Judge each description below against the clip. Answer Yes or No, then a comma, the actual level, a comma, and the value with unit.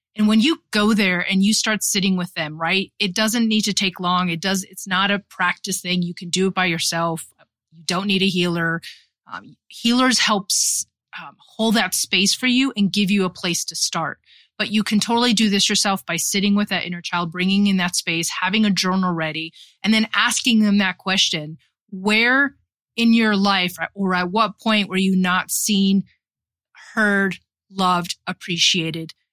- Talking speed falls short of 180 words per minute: No, average, 190 wpm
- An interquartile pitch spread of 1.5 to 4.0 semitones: Yes, average, 3.0 semitones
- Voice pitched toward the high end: Yes, high, 195 Hz